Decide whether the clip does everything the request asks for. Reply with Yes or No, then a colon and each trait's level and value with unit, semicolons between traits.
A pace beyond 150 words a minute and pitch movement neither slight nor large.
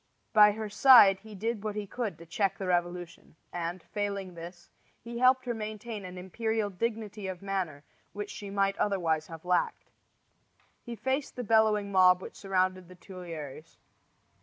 Yes: average, 165 wpm; average, 3.2 semitones